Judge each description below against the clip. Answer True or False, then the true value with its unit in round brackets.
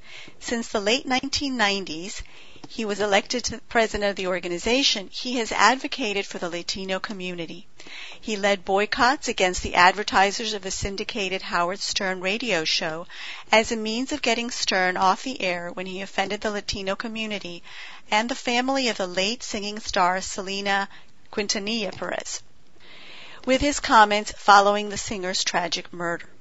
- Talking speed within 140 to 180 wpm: True (150 wpm)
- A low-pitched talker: False (205 Hz)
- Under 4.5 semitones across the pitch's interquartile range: True (3.3 semitones)